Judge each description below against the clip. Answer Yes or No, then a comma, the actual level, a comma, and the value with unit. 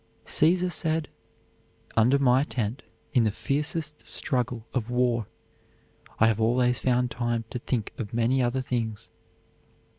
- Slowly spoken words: Yes, slow, 130 wpm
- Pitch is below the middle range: Yes, low, 125 Hz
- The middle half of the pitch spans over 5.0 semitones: No, average, 3.0 semitones